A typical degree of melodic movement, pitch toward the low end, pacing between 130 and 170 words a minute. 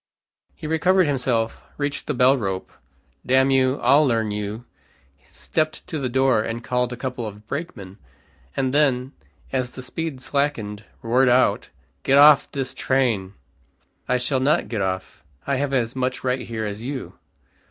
Yes: average, 3.3 semitones; low, 130 Hz; average, 160 wpm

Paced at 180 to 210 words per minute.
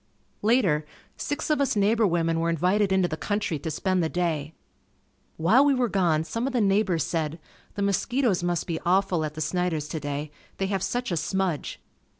Yes: average, 185 wpm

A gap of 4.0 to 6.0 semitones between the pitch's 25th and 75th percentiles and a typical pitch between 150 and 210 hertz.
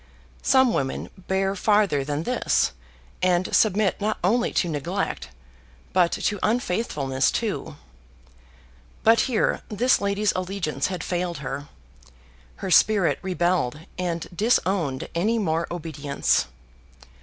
Yes: average, 4.9 semitones; medium, 185 Hz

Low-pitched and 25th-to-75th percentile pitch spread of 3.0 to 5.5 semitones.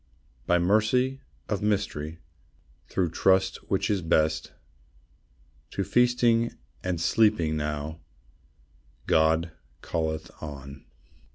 Yes: very low, 85 Hz; average, 5.1 semitones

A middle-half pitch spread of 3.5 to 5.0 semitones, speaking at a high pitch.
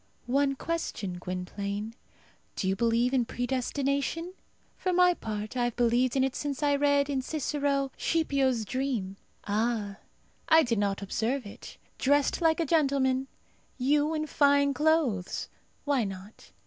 Yes: average, 4.4 semitones; very high, 265 Hz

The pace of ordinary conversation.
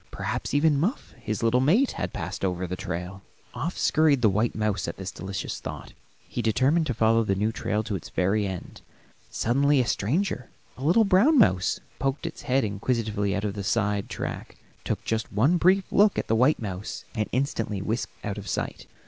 Yes: average, 195 wpm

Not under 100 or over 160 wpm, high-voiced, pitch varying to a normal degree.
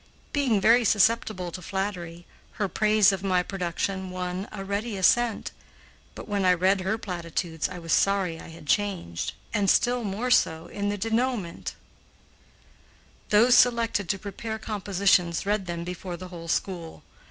Yes: average, 155 wpm; high, 195 Hz; average, 3.1 semitones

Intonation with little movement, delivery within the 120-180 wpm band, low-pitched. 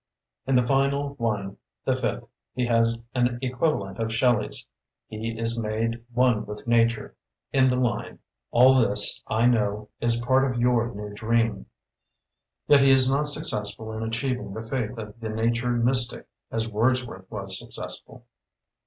Yes: narrow, 2.3 semitones; average, 155 wpm; low, 115 Hz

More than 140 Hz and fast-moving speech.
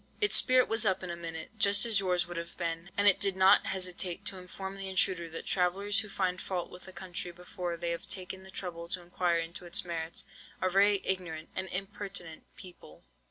Yes: medium, 185 Hz; fast, 210 wpm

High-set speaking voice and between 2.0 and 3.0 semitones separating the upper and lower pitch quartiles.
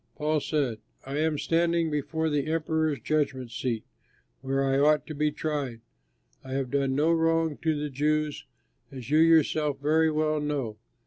No: medium, 150 Hz; narrow, 2.4 semitones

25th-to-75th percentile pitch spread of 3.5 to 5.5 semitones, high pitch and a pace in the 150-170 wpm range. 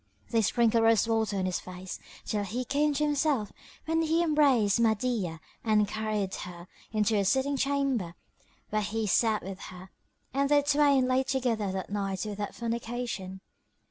Yes: average, 4.9 semitones; high, 225 Hz; average, 160 wpm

